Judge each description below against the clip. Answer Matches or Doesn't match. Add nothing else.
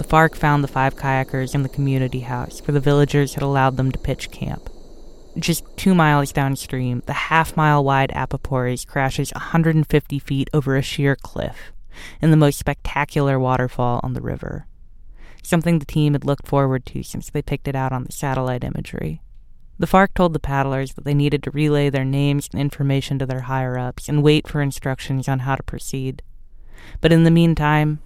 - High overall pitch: Doesn't match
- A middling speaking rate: Matches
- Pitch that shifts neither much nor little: Doesn't match